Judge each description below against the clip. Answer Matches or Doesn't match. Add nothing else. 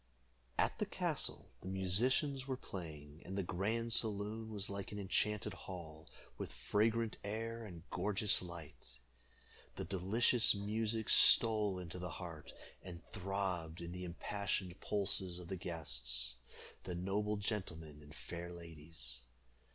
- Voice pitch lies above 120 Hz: Doesn't match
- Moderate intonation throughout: Matches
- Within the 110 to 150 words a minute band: Matches